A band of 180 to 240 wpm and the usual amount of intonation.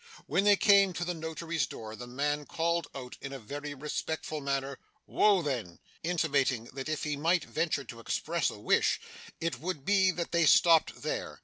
Yes: average, 185 wpm; average, 3.8 semitones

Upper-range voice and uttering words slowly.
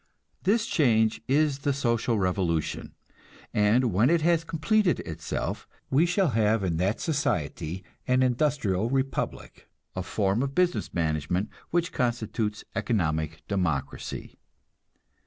No: low, 115 Hz; slow, 120 wpm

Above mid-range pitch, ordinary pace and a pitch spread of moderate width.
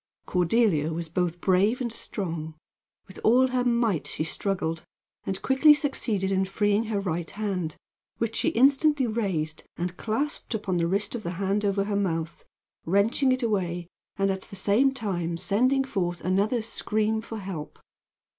Yes: high, 200 Hz; average, 160 wpm; average, 4.5 semitones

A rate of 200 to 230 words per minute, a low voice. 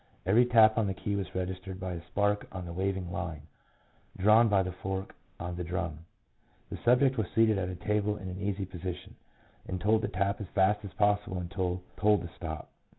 Yes: fast, 205 wpm; very low, 95 Hz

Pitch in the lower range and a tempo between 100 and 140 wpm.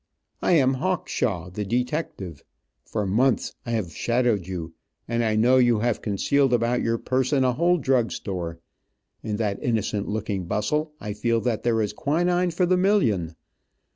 No: low, 115 Hz; average, 165 wpm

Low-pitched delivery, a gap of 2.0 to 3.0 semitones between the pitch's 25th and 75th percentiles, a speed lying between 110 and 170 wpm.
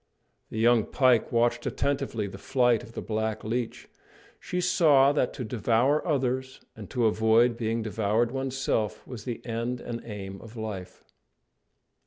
Yes: low, 115 Hz; narrow, 2.6 semitones; average, 150 wpm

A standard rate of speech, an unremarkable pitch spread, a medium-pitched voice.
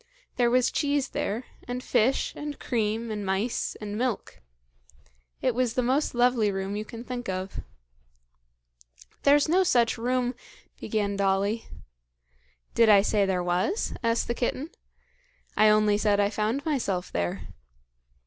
No: average, 145 wpm; average, 3.7 semitones; high, 230 Hz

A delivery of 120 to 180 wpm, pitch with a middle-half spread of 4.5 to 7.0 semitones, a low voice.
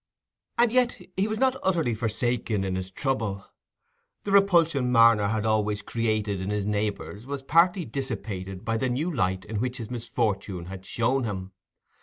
Yes: average, 165 wpm; average, 5.1 semitones; low, 115 Hz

